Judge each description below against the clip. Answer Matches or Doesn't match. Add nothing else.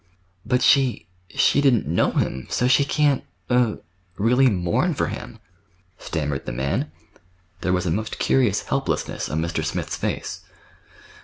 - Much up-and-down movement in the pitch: Matches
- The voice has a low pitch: Matches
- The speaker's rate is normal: Doesn't match